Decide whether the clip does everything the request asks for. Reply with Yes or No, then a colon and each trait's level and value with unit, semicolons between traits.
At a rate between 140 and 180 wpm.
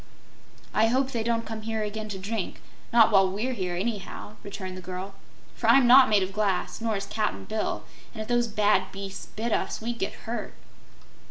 No: average, 195 wpm